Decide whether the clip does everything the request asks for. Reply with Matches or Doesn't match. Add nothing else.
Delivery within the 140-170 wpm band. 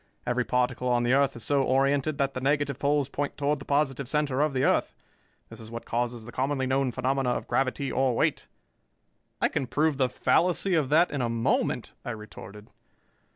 Doesn't match